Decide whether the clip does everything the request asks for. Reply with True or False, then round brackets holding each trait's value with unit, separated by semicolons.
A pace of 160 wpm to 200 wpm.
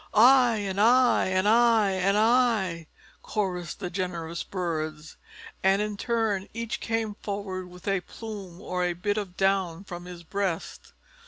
False (150 wpm)